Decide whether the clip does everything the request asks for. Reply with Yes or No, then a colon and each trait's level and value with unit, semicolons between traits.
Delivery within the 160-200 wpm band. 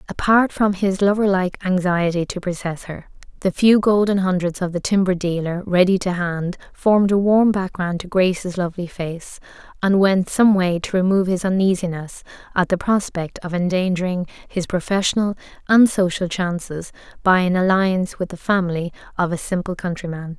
Yes: average, 165 wpm